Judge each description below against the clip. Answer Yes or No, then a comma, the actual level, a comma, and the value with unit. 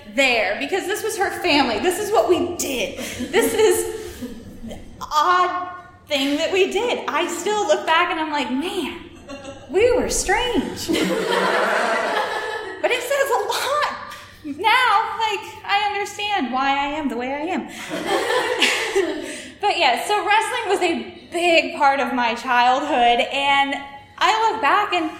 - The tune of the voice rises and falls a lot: Yes, wide, 6.6 semitones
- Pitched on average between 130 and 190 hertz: No, very high, 350 Hz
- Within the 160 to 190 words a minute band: No, average, 150 wpm